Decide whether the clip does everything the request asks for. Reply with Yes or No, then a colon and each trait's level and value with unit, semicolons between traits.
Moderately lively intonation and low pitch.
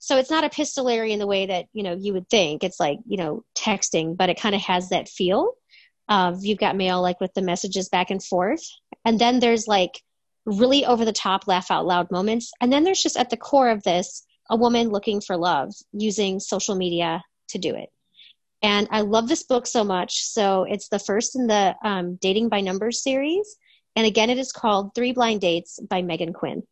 No: average, 4.2 semitones; high, 210 Hz